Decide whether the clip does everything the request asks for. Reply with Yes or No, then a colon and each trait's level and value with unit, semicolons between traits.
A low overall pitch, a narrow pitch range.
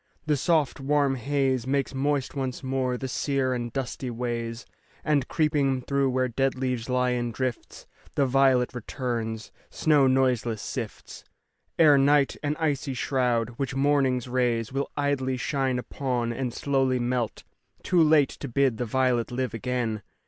Yes: low, 130 Hz; narrow, 2.1 semitones